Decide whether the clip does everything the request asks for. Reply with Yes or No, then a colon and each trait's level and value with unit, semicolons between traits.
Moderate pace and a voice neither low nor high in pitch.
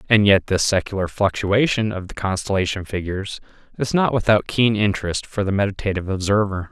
No: average, 160 wpm; low, 100 Hz